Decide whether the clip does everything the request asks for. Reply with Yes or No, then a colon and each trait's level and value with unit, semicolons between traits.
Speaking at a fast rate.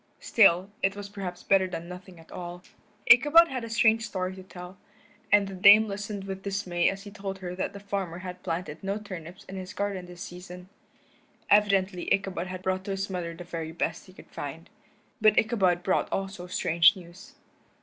No: average, 190 wpm